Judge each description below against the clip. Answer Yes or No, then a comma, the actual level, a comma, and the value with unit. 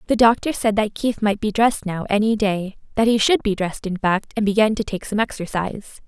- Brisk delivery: Yes, fast, 225 wpm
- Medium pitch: No, high, 210 Hz